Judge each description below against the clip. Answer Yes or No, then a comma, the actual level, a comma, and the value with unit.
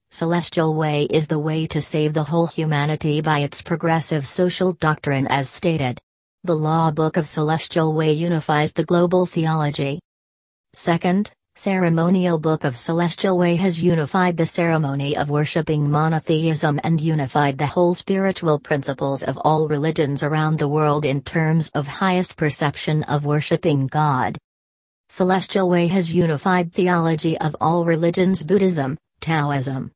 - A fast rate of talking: No, average, 140 wpm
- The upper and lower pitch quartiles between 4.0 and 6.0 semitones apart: No, narrow, 2.6 semitones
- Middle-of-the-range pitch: Yes, medium, 160 Hz